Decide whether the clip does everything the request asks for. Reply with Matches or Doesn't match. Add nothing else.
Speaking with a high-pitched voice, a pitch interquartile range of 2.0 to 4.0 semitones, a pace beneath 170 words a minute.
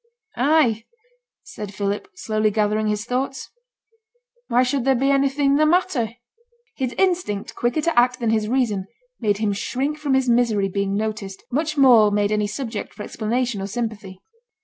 Doesn't match